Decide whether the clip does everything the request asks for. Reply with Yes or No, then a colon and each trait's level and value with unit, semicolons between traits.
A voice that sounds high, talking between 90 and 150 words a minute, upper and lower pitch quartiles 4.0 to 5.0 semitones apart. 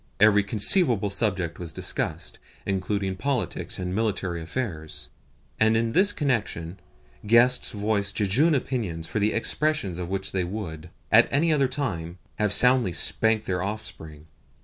No: low, 105 Hz; average, 140 wpm; average, 4.6 semitones